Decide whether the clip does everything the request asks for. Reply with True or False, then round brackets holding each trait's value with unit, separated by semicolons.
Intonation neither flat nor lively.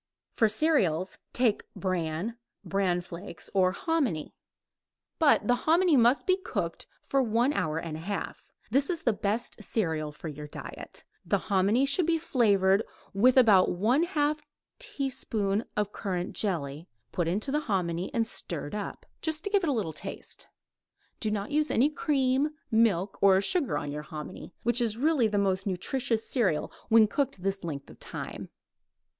False (6.7 semitones)